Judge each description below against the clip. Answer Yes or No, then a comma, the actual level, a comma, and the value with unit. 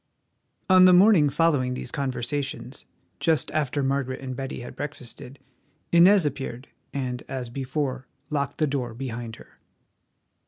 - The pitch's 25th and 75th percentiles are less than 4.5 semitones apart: Yes, average, 2.9 semitones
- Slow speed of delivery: Yes, slow, 130 wpm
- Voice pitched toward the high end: No, low, 135 Hz